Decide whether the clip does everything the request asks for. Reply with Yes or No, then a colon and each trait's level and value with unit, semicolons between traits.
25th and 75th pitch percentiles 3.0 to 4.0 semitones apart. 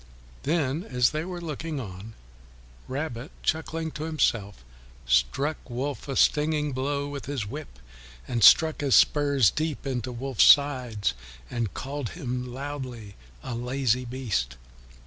Yes: average, 3.7 semitones